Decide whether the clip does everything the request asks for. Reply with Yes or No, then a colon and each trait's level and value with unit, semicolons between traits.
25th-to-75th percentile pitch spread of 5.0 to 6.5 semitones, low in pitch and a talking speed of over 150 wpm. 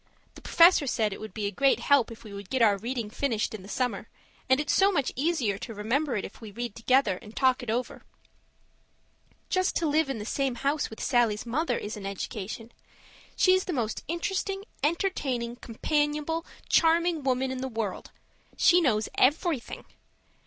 No: wide, 5.6 semitones; very high, 255 Hz; average, 180 wpm